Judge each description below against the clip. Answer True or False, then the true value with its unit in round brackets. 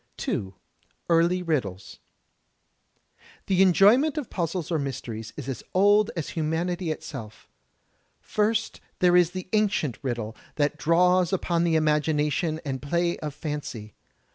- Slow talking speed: True (125 wpm)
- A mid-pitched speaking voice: True (165 Hz)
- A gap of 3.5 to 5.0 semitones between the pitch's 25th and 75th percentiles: True (4.4 semitones)